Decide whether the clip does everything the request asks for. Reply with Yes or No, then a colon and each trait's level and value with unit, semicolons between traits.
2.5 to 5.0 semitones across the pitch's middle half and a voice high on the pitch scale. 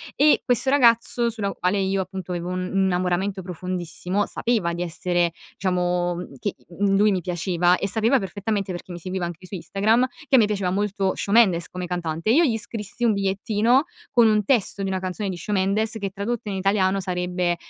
Yes: average, 2.9 semitones; high, 195 Hz